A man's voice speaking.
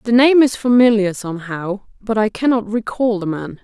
No: female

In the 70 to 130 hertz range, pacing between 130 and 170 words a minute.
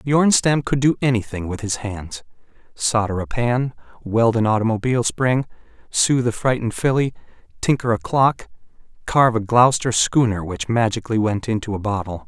Yes: low, 115 Hz; average, 145 wpm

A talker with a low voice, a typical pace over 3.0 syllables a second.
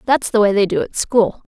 No: high, 215 Hz; 5.3 syllables/s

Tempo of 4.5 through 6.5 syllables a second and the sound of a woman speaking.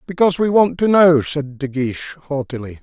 No: 5.2 syllables/s; male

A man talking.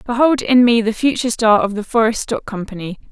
No: female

